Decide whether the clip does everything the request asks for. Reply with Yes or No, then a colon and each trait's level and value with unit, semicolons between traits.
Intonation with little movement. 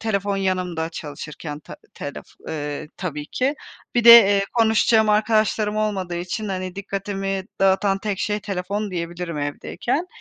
No: average, 3.5 semitones